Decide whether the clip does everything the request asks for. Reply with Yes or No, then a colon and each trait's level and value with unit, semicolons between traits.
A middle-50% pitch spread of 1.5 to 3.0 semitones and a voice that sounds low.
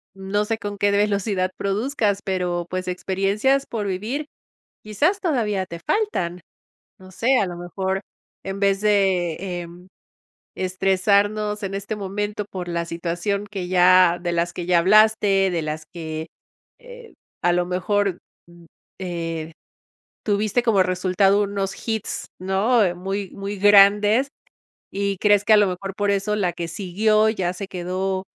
No: narrow, 2.4 semitones; high, 195 Hz